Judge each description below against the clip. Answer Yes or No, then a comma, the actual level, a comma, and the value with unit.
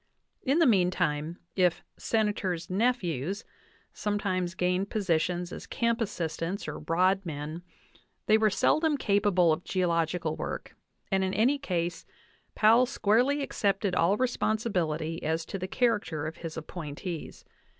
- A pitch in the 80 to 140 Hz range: No, medium, 185 Hz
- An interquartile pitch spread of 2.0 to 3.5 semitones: No, average, 4.4 semitones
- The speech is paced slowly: Yes, slow, 125 wpm